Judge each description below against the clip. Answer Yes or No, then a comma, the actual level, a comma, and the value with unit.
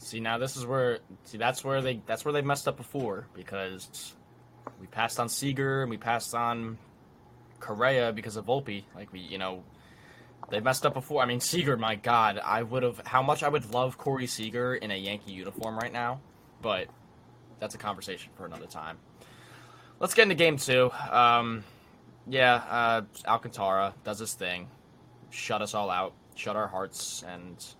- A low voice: Yes, low, 120 Hz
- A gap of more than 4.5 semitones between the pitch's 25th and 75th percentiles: No, average, 3.4 semitones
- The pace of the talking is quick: No, average, 180 wpm